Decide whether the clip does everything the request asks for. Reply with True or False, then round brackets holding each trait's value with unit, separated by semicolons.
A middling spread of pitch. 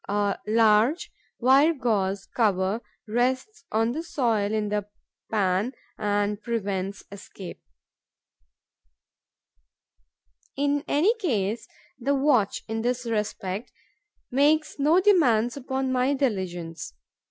True (5.0 semitones)